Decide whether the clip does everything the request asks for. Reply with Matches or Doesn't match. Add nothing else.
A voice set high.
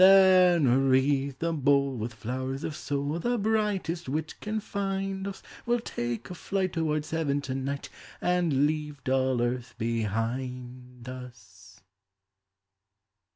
Doesn't match